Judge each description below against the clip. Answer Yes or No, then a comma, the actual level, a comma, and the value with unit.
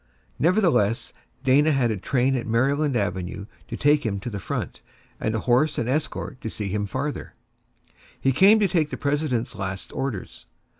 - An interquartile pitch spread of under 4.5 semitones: No, wide, 5.4 semitones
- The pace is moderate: Yes, average, 170 wpm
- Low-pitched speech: Yes, low, 130 Hz